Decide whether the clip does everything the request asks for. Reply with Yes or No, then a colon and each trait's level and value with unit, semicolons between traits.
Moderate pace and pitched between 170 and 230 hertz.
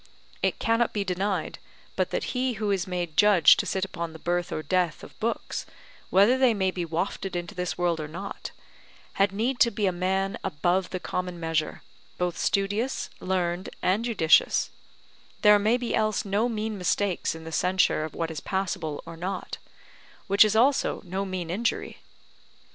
Yes: average, 175 wpm; high, 190 Hz